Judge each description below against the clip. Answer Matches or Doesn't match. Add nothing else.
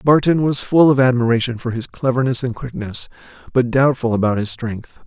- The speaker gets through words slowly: Doesn't match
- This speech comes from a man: Matches